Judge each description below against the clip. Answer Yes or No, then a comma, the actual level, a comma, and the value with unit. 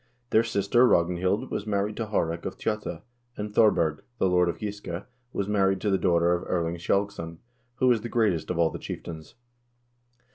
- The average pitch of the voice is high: No, very low, 95 Hz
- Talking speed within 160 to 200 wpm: Yes, average, 180 wpm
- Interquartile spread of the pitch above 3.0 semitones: Yes, average, 3.7 semitones